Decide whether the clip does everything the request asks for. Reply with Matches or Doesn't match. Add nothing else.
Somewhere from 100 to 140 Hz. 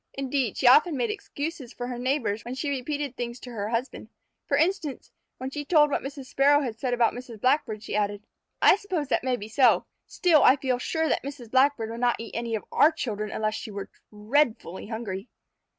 Doesn't match